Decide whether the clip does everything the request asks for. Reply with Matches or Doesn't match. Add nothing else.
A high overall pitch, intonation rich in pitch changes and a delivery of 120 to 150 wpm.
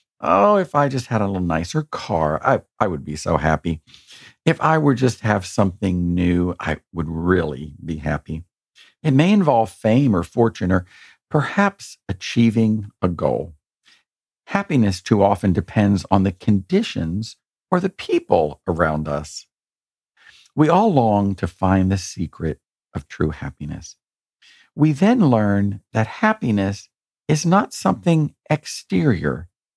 Doesn't match